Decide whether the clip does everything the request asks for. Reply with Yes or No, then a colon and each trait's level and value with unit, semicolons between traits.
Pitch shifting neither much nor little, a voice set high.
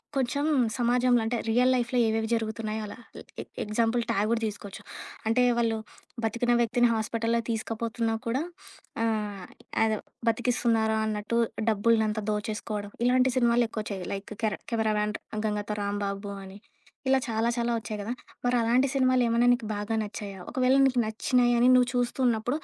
No: narrow, 2.2 semitones; high, 225 Hz